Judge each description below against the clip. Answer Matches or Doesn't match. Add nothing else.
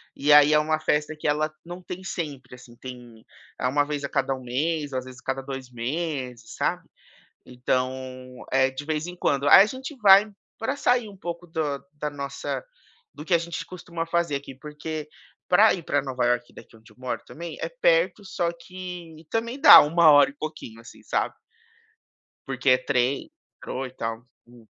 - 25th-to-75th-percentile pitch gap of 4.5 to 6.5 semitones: Matches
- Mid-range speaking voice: Matches